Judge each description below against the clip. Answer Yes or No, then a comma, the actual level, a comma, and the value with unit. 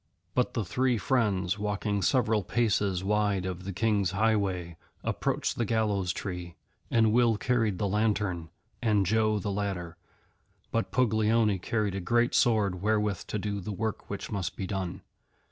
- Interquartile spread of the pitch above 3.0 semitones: No, average, 2.7 semitones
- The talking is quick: No, average, 155 wpm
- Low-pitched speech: Yes, low, 105 Hz